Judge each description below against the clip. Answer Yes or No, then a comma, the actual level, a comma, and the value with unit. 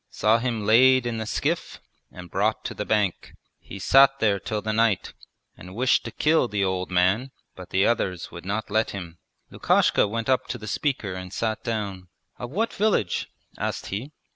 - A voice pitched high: No, low, 110 Hz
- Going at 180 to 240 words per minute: Yes, average, 190 wpm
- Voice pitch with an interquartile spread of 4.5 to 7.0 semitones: No, average, 4.1 semitones